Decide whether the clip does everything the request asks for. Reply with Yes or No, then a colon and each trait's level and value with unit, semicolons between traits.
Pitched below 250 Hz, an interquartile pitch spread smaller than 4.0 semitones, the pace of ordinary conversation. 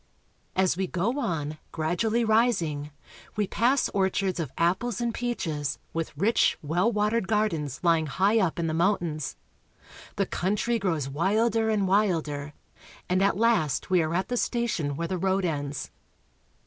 No: medium, 185 Hz; average, 5.3 semitones; average, 150 wpm